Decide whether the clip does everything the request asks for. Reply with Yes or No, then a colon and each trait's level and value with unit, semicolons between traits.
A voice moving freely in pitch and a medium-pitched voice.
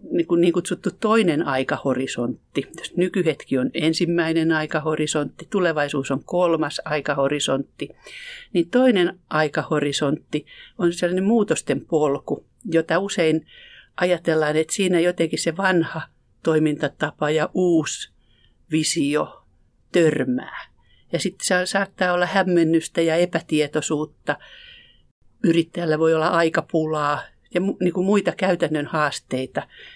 No: average, 2.7 semitones; medium, 165 Hz